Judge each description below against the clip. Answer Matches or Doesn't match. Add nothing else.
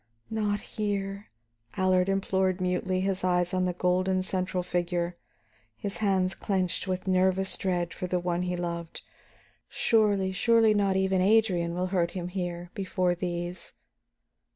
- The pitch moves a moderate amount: Doesn't match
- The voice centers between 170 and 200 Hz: Matches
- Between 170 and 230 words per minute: Doesn't match